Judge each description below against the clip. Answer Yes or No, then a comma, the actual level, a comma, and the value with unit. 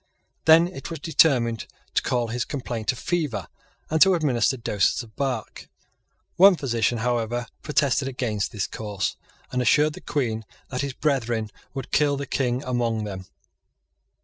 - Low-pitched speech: Yes, low, 125 Hz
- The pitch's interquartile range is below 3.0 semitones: No, average, 3.9 semitones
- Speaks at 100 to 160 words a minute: Yes, average, 150 wpm